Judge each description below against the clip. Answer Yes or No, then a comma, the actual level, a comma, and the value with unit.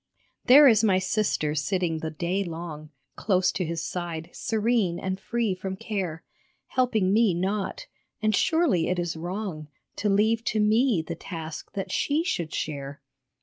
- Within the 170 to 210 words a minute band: No, average, 155 wpm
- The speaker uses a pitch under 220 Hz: Yes, medium, 185 Hz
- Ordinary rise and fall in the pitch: Yes, average, 4.4 semitones